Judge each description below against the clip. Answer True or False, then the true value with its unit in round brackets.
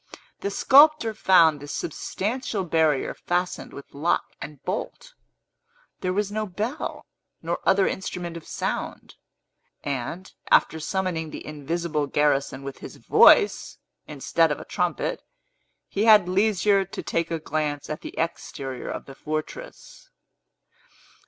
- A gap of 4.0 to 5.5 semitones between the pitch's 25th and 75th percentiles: True (5.0 semitones)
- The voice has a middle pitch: True (175 Hz)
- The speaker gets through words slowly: True (130 wpm)